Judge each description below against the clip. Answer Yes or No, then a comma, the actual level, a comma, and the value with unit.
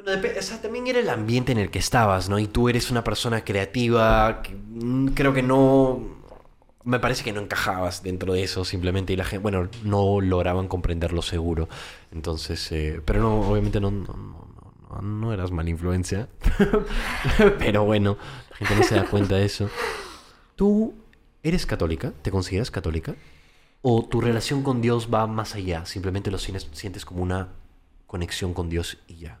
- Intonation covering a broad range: No, average, 4.4 semitones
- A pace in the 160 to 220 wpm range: Yes, average, 175 wpm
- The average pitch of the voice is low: Yes, low, 100 Hz